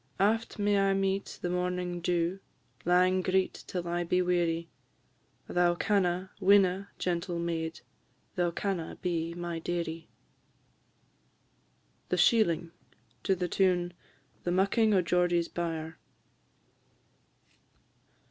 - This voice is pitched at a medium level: Yes, medium, 180 Hz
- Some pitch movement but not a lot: No, narrow, 1.9 semitones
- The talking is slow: Yes, slow, 100 wpm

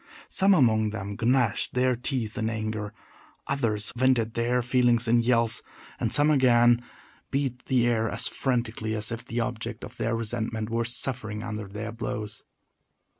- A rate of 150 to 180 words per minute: Yes, average, 155 wpm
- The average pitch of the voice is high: No, low, 115 Hz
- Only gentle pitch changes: Yes, narrow, 2.3 semitones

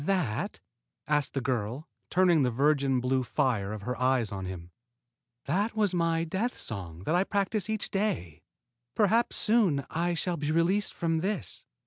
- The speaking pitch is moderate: Yes, medium, 155 Hz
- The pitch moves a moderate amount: No, wide, 7.2 semitones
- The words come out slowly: No, average, 160 wpm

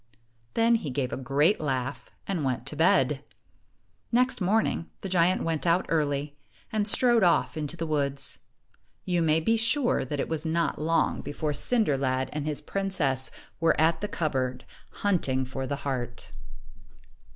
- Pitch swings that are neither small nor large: Yes, average, 4.9 semitones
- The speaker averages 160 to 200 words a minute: Yes, average, 165 wpm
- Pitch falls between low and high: Yes, medium, 155 Hz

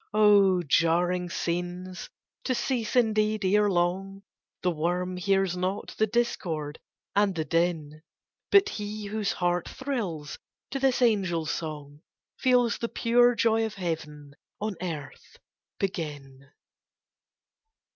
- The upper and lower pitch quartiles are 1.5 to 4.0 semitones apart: No, average, 4.4 semitones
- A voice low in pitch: No, medium, 185 Hz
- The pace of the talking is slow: Yes, slow, 115 wpm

